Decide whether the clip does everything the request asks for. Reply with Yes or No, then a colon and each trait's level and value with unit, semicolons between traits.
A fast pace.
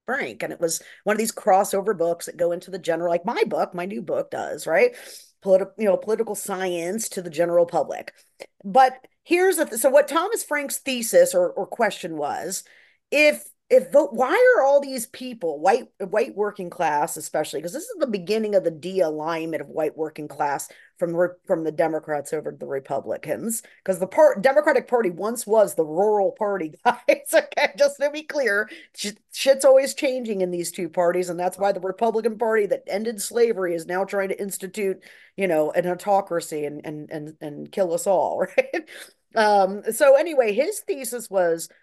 No: average, 190 wpm